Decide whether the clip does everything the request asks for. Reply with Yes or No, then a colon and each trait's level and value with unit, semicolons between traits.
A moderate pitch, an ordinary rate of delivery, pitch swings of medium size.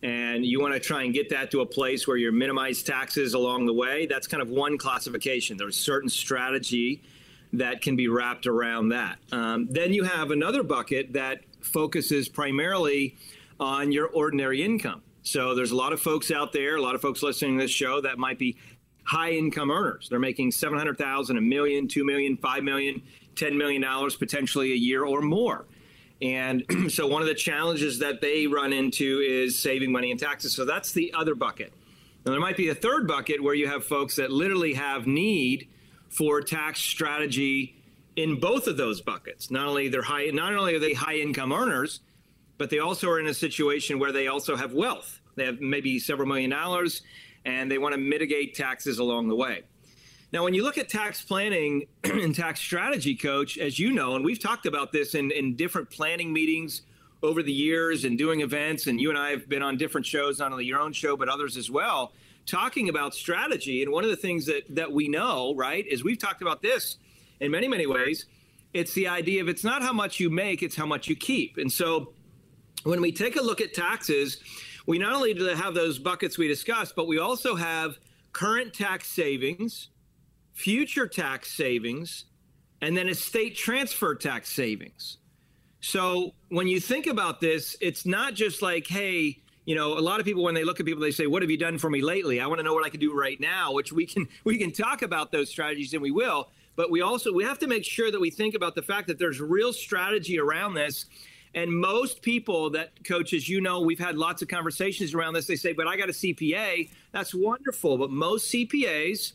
No: medium, 155 Hz; fast, 210 wpm; average, 4.2 semitones